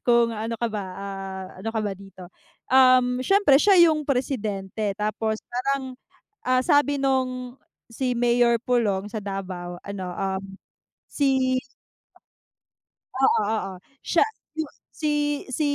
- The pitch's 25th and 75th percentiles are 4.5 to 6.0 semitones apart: Yes, average, 4.9 semitones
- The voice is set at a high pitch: Yes, high, 240 Hz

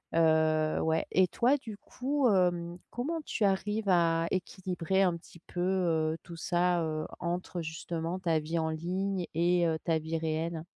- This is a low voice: No, medium, 175 Hz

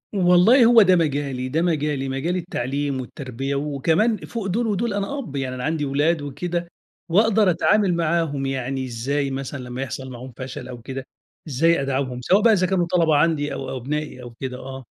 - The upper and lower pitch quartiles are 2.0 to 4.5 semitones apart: No, average, 5.0 semitones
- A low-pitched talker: No, medium, 145 Hz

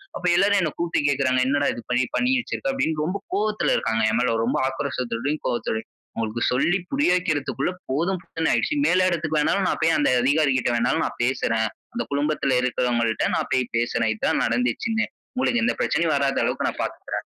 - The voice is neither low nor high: Yes, medium, 145 Hz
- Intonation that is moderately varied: No, wide, 6.0 semitones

